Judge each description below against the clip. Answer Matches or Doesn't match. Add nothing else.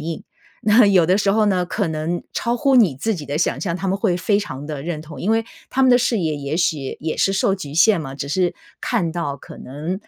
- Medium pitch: Matches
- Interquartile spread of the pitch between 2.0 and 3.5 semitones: Doesn't match